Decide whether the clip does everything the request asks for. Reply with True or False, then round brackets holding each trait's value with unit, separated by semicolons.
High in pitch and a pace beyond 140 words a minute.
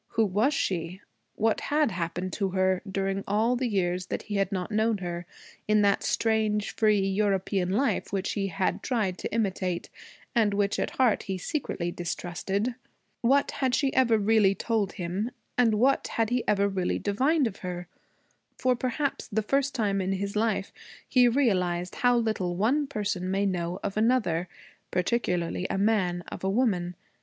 True (200 Hz; 170 wpm)